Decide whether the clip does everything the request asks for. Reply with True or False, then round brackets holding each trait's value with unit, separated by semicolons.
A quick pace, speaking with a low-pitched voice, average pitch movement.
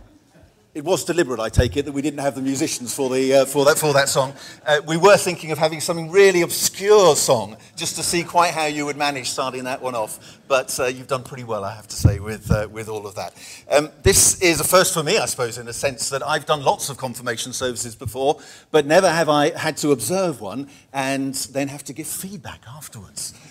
False (235 wpm; 145 Hz; 4.1 semitones)